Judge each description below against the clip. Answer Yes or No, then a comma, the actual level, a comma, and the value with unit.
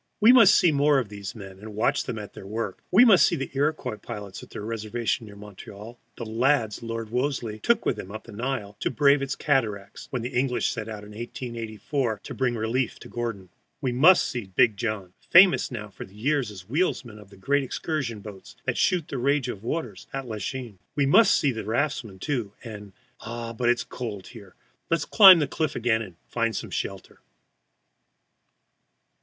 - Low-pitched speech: Yes, low, 115 Hz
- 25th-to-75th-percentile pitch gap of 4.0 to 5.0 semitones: Yes, average, 4.6 semitones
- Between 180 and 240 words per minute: Yes, average, 200 wpm